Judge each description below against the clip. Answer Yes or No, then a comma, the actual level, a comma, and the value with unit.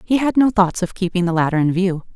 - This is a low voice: No, high, 190 Hz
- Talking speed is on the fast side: Yes, fast, 280 wpm